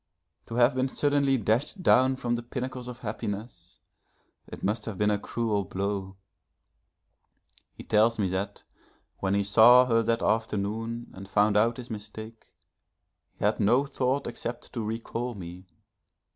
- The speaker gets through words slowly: No, average, 150 wpm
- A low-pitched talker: Yes, low, 115 Hz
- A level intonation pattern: No, average, 3.1 semitones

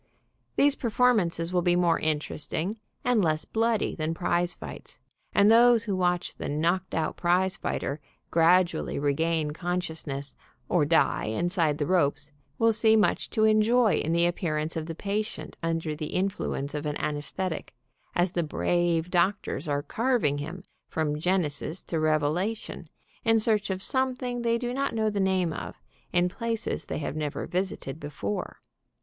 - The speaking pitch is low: No, medium, 175 Hz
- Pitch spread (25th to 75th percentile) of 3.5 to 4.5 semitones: No, average, 5.3 semitones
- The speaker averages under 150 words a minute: No, average, 160 wpm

